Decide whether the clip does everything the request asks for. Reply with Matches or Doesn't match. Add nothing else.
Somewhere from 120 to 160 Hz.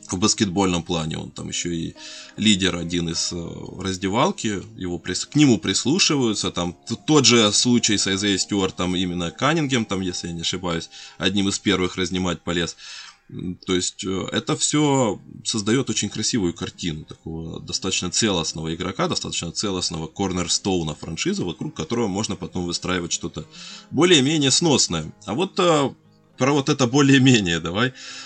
Doesn't match